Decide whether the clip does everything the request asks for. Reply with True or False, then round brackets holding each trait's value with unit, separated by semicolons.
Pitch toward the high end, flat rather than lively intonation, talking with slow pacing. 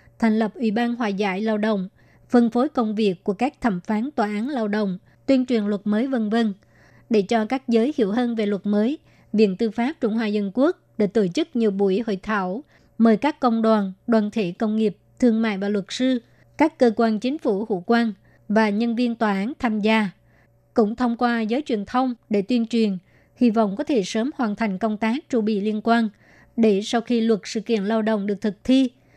False (225 Hz; 2.2 semitones; 225 wpm)